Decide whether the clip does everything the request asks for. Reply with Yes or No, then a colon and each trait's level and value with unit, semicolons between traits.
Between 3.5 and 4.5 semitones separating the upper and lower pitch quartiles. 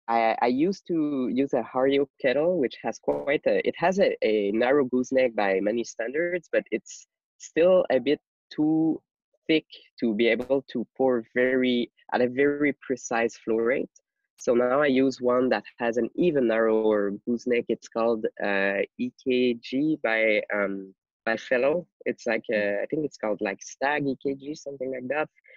Yes: average, 4.0 semitones